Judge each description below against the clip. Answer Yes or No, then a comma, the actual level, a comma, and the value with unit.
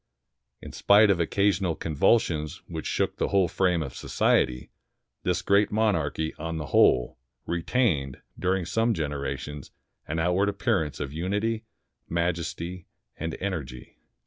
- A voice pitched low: Yes, very low, 85 Hz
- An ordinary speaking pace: No, slow, 125 wpm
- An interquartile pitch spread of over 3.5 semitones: Yes, average, 4.7 semitones